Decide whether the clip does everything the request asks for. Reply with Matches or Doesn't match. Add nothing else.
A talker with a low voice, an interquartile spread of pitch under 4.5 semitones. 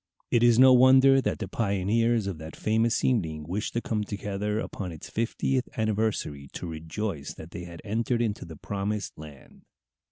Doesn't match